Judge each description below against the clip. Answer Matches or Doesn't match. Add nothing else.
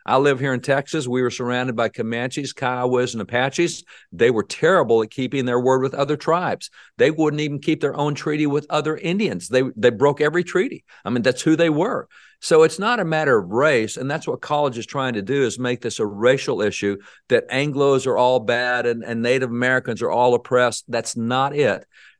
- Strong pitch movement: Doesn't match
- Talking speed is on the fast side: Matches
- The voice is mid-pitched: Doesn't match